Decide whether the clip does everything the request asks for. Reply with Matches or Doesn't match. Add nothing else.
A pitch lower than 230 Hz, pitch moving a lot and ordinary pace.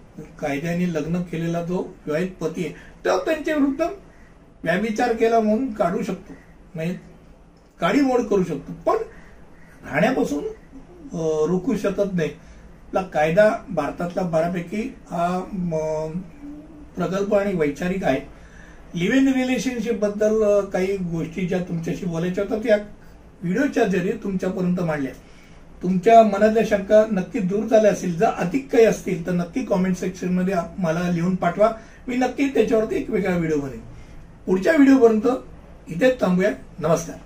Doesn't match